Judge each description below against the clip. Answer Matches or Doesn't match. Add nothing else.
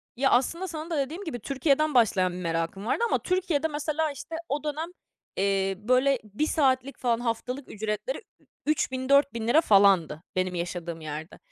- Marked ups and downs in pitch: Matches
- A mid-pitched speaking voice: Doesn't match